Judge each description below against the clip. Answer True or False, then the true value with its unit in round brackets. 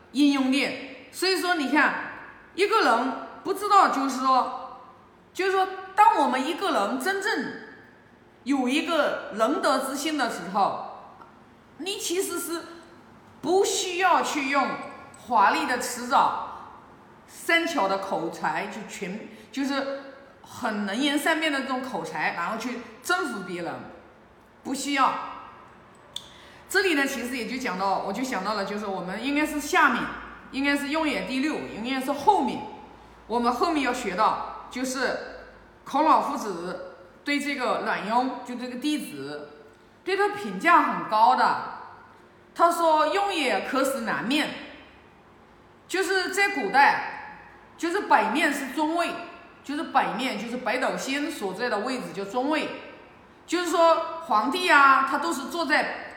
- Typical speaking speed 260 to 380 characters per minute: False (205 characters per minute)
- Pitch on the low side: False (280 Hz)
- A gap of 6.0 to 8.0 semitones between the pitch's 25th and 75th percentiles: False (5.6 semitones)